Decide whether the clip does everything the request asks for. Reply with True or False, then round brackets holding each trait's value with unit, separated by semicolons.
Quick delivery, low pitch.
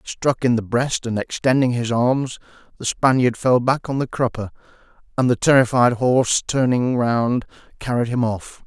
False (165 wpm; 125 Hz)